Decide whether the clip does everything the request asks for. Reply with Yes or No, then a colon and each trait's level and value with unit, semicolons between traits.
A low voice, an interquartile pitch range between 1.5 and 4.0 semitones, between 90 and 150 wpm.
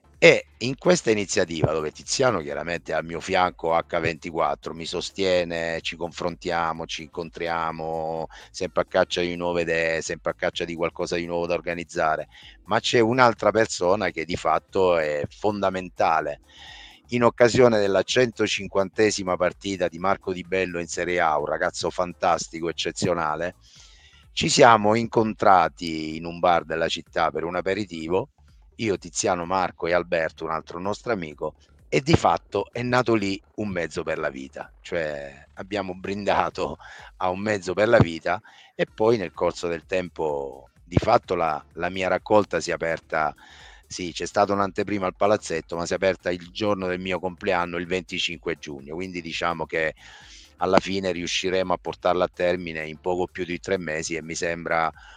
No: very low, 90 Hz; average, 3.0 semitones; average, 165 wpm